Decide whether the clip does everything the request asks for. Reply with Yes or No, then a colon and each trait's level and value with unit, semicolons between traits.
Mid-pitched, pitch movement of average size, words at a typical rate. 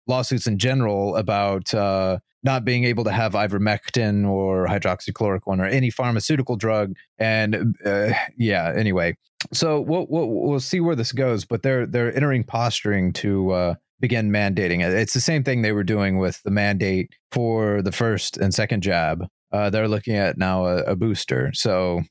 No: low, 110 Hz; average, 3.7 semitones; average, 175 wpm